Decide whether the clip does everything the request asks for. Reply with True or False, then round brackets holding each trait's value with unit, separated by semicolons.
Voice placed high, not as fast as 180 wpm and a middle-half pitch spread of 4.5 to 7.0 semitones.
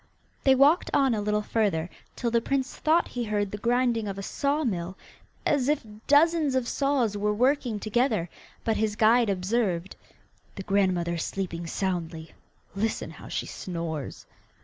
True (215 Hz; 160 wpm; 5.2 semitones)